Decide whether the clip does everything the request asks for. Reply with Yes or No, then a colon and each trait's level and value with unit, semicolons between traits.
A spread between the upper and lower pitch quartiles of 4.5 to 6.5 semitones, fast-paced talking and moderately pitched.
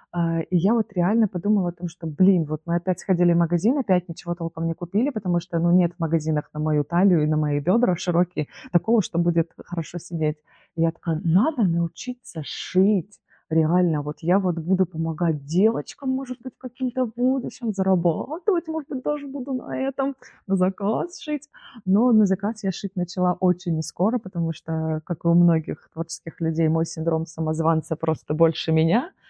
Yes: average, 4.8 semitones; fast, 180 wpm; medium, 175 Hz